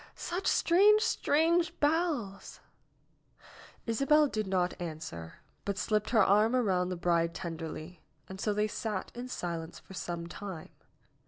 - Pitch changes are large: Yes, wide, 7.6 semitones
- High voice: Yes, high, 200 Hz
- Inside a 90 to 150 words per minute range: Yes, average, 140 wpm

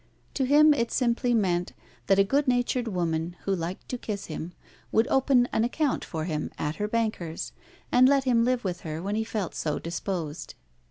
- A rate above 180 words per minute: Yes, average, 195 wpm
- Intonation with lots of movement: Yes, wide, 6.2 semitones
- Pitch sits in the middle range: No, high, 210 Hz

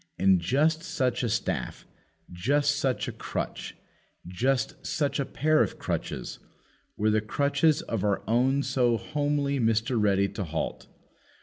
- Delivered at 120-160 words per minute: Yes, average, 140 wpm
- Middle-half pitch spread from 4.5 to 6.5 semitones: Yes, average, 4.9 semitones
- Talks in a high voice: No, low, 125 Hz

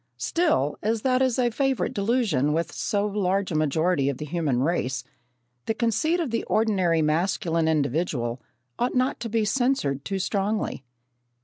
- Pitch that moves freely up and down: Yes, wide, 7.0 semitones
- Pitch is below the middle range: No, high, 190 Hz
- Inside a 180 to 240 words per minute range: No, average, 155 wpm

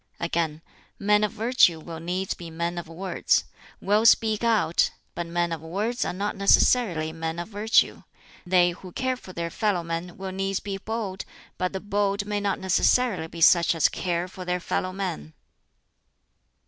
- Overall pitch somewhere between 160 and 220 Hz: Yes, medium, 185 Hz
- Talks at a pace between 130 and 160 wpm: No, average, 175 wpm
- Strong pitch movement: No, average, 3.3 semitones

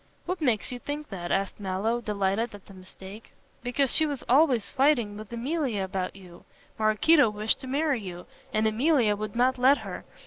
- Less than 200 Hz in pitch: No, high, 225 Hz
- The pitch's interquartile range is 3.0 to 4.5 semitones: No, average, 5.2 semitones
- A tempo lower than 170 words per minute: No, average, 180 wpm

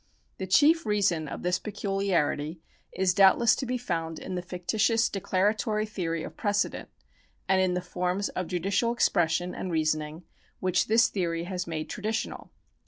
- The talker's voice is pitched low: No, medium, 185 Hz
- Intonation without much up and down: No, average, 3.2 semitones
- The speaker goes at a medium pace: Yes, average, 160 wpm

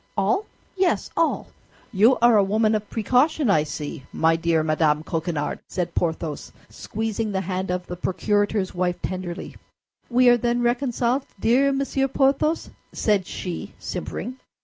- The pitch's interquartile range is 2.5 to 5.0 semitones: No, wide, 5.6 semitones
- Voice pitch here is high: Yes, high, 205 Hz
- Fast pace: No, average, 145 wpm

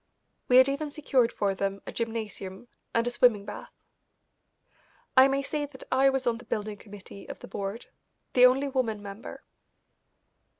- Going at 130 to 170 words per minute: Yes, average, 165 wpm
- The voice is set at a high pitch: Yes, high, 240 Hz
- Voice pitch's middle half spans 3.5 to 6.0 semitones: Yes, average, 4.4 semitones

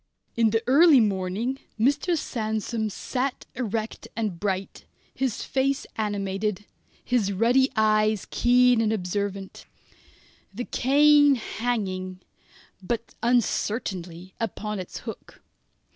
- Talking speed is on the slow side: Yes, slow, 100 wpm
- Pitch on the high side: Yes, high, 220 Hz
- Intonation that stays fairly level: No, average, 3.9 semitones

